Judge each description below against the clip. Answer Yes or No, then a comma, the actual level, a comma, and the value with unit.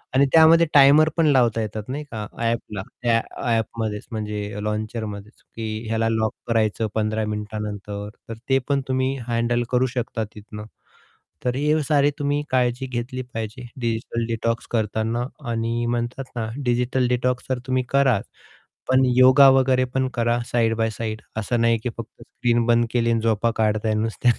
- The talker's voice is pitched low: Yes, low, 115 Hz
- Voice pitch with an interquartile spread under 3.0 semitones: Yes, narrow, 2.6 semitones